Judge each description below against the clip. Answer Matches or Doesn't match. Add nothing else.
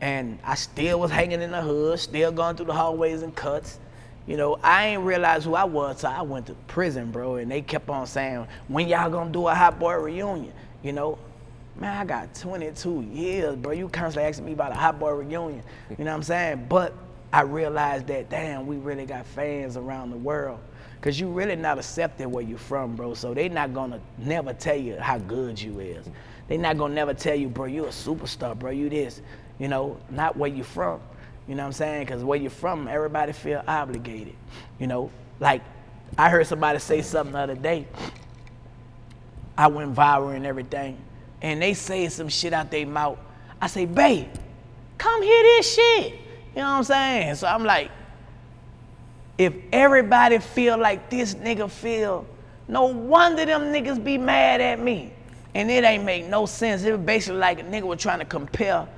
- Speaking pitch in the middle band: Matches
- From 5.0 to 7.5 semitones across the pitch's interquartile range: Matches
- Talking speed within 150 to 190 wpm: Doesn't match